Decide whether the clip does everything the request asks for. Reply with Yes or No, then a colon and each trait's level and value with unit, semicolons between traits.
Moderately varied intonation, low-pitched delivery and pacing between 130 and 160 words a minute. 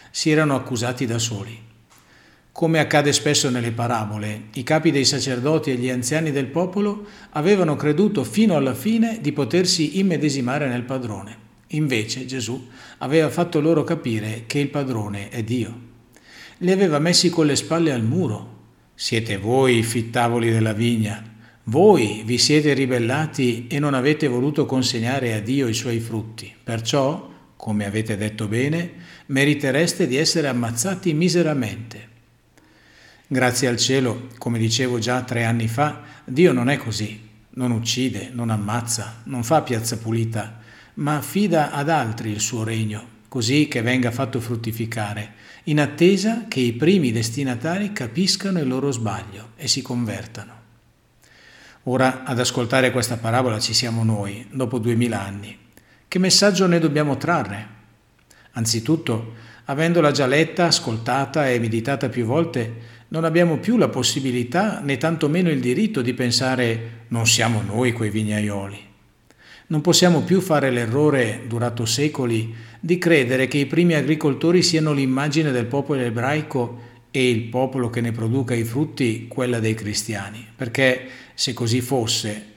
Yes: average, 4.5 semitones; low, 125 Hz; average, 145 wpm